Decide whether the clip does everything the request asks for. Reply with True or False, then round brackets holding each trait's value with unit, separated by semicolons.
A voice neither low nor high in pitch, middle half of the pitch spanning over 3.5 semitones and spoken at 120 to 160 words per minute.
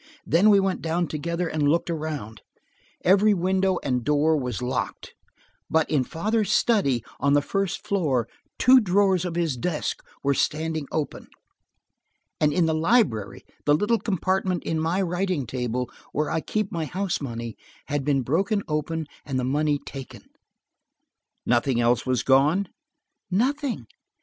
True (160 Hz; 5.4 semitones; 150 wpm)